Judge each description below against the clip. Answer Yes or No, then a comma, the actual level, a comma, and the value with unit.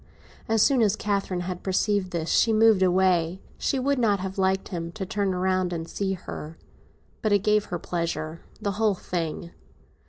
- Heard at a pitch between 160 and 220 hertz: Yes, high, 190 Hz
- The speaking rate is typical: Yes, average, 175 wpm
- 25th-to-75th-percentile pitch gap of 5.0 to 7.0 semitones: No, average, 2.9 semitones